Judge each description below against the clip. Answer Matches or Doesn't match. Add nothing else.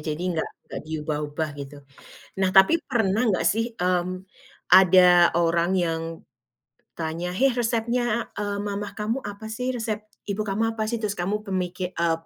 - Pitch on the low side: Doesn't match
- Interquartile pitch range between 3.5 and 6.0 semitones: Matches